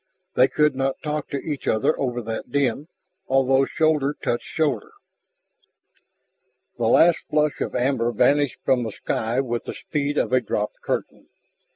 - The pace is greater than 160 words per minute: No, average, 155 wpm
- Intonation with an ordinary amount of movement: Yes, average, 3.4 semitones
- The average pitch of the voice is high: No, low, 135 Hz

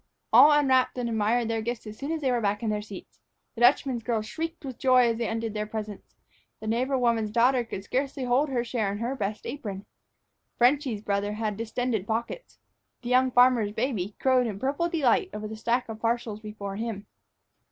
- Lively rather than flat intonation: No, average, 3.1 semitones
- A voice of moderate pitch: No, high, 235 Hz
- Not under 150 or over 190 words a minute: No, average, 200 wpm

